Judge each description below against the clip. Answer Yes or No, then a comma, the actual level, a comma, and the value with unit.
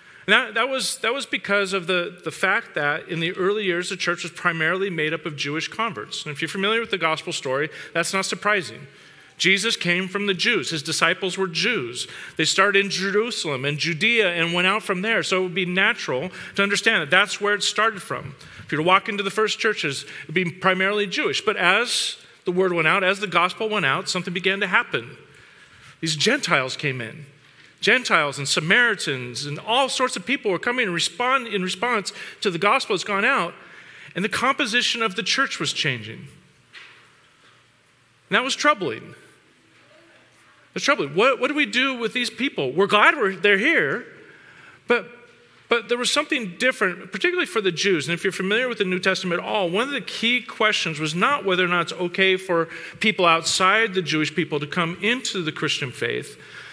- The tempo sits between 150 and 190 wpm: No, fast, 205 wpm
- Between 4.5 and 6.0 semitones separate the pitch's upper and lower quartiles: Yes, average, 5.0 semitones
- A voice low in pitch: No, high, 190 Hz